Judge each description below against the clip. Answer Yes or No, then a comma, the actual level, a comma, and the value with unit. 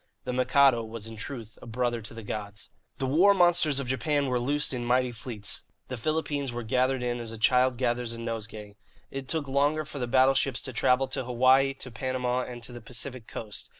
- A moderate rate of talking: No, fast, 210 wpm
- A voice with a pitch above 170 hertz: No, low, 125 Hz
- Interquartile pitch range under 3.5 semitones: Yes, narrow, 2.5 semitones